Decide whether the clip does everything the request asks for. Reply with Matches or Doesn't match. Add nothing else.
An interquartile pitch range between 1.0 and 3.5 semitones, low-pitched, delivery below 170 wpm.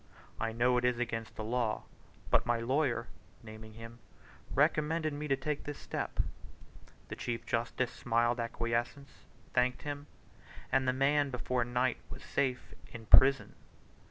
Matches